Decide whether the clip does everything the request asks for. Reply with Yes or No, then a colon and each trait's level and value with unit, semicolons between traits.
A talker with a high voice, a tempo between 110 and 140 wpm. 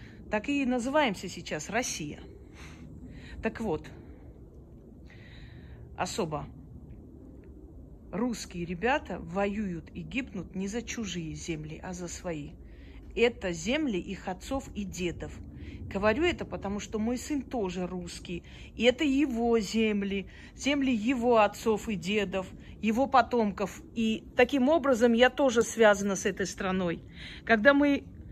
Yes: high, 205 Hz; average, 120 wpm